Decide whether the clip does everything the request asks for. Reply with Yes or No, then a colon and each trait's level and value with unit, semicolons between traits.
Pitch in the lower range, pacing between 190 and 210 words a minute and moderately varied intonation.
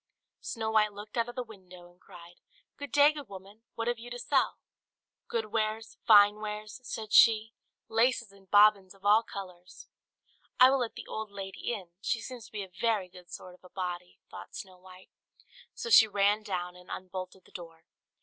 No: high, 210 Hz; average, 195 wpm; average, 3.5 semitones